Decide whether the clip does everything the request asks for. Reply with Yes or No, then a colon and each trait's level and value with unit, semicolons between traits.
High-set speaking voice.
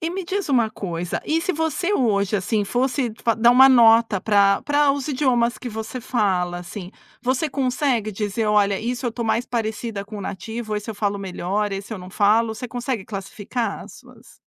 Yes: high, 225 Hz